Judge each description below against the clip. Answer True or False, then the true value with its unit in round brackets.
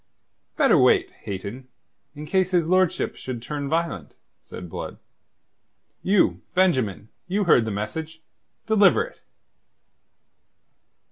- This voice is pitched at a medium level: True (155 Hz)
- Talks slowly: True (110 wpm)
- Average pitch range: False (8.7 semitones)